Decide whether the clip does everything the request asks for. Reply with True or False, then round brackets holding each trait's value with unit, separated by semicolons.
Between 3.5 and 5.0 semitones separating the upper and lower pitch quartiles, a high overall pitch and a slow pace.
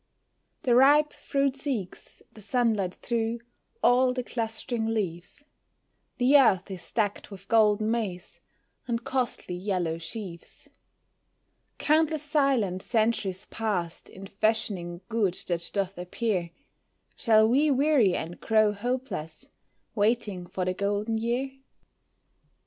True (4.6 semitones; 220 Hz; 115 wpm)